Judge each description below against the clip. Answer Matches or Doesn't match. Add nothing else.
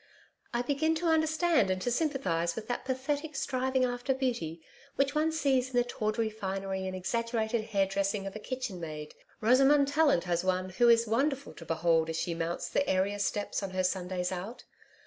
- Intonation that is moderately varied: Doesn't match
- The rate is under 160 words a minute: Doesn't match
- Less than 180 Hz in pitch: Doesn't match